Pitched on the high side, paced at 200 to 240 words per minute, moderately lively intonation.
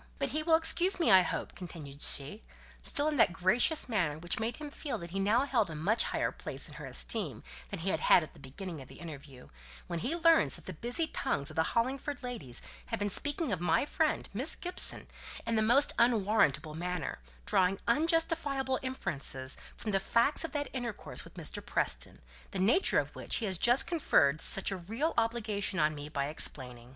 No: high, 215 Hz; fast, 205 wpm; wide, 8.6 semitones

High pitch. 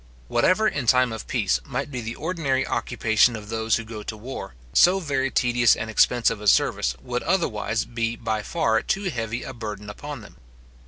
No: low, 115 Hz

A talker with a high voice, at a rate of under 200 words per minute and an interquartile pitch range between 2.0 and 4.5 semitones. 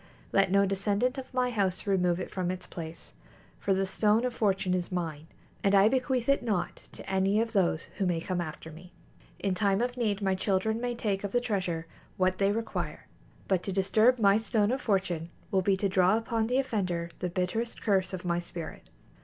No: high, 195 Hz; fast, 205 wpm; average, 3.5 semitones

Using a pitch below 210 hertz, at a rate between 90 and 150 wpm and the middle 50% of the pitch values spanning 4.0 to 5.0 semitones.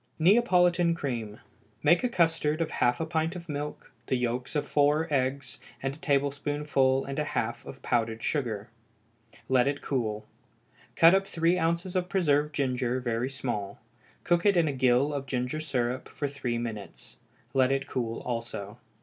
No: medium, 140 Hz; average, 165 wpm; average, 4.7 semitones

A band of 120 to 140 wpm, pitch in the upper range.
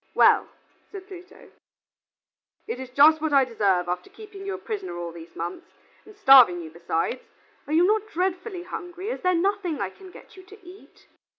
No: average, 185 wpm; very high, 355 Hz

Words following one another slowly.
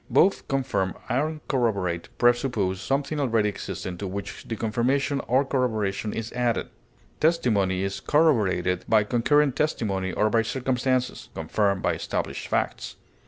Yes: slow, 130 wpm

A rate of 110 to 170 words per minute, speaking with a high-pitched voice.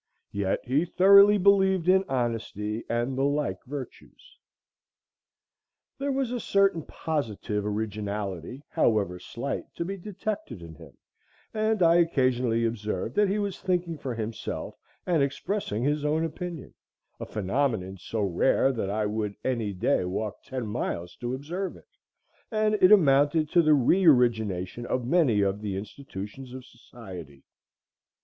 No: average, 140 wpm; low, 130 Hz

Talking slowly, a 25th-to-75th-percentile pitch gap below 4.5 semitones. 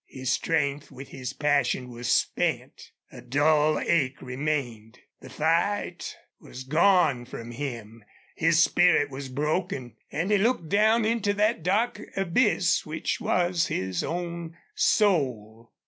No: slow, 130 wpm; wide, 5.6 semitones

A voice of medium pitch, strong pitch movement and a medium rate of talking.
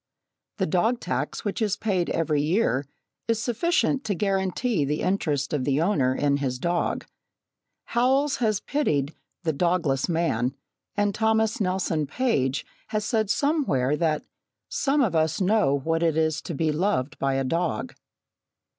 Yes: medium, 170 Hz; wide, 6.9 semitones; average, 150 wpm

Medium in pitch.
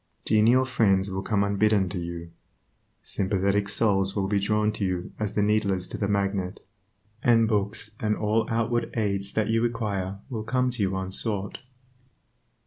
No: low, 100 Hz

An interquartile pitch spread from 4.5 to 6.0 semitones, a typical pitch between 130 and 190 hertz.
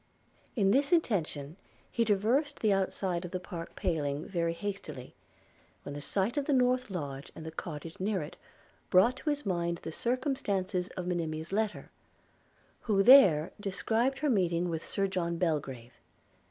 Yes: average, 5.2 semitones; medium, 185 Hz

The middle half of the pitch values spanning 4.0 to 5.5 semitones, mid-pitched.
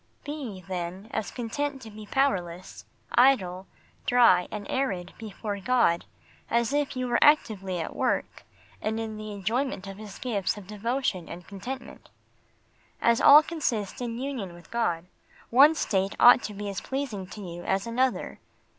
No: average, 4.8 semitones; high, 215 Hz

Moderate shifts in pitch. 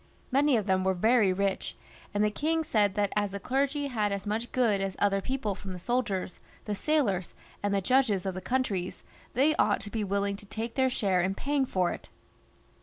Yes: average, 4.6 semitones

